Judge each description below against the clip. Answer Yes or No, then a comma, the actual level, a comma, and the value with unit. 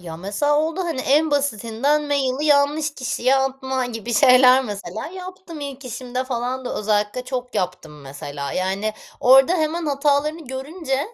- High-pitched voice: Yes, very high, 265 Hz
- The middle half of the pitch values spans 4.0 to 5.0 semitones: Yes, average, 4.3 semitones